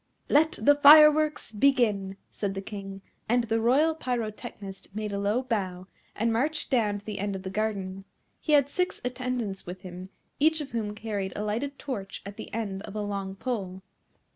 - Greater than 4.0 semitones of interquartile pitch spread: Yes, average, 4.6 semitones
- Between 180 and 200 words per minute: Yes, average, 185 wpm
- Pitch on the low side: No, high, 215 Hz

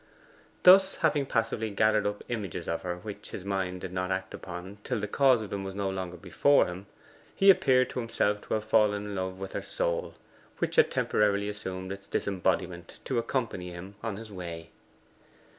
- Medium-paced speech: Yes, average, 190 wpm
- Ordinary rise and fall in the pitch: Yes, average, 3.0 semitones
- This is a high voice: No, low, 100 Hz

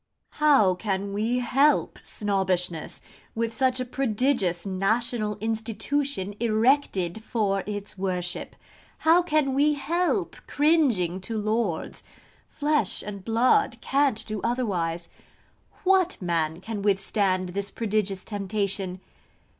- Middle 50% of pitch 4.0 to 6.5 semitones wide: Yes, average, 5.1 semitones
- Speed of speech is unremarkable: No, slow, 105 wpm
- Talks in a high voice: Yes, high, 215 Hz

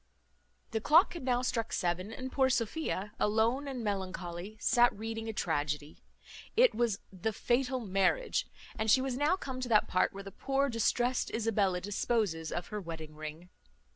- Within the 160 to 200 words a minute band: Yes, average, 170 wpm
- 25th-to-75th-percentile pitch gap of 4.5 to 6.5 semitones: Yes, average, 5.3 semitones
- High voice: Yes, high, 220 Hz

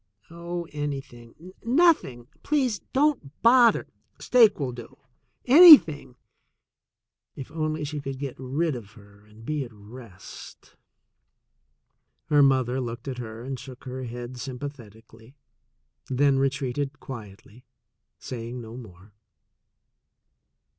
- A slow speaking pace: Yes, slow, 125 wpm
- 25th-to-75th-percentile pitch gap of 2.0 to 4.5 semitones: Yes, average, 4.1 semitones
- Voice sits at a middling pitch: No, low, 130 Hz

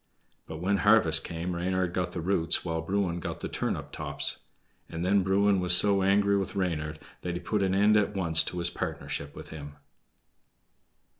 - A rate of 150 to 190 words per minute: Yes, average, 180 wpm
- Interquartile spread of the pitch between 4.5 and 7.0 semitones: No, average, 2.9 semitones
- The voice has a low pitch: Yes, very low, 90 Hz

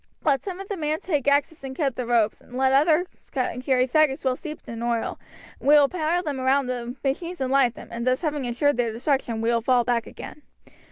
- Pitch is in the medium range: No, very high, 265 Hz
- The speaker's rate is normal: No, fast, 225 wpm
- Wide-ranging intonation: No, average, 3.6 semitones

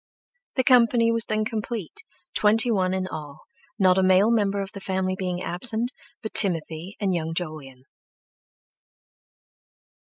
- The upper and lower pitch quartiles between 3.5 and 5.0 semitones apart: Yes, average, 3.8 semitones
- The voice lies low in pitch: No, high, 190 Hz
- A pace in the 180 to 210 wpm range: No, slow, 135 wpm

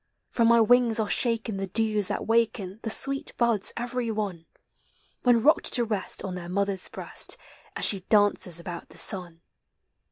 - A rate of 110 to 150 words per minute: No, average, 165 wpm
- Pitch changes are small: No, average, 3.5 semitones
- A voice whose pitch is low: No, high, 215 Hz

